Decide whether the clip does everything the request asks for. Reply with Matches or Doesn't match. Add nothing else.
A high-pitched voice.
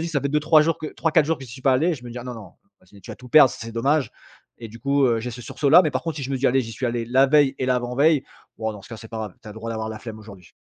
Doesn't match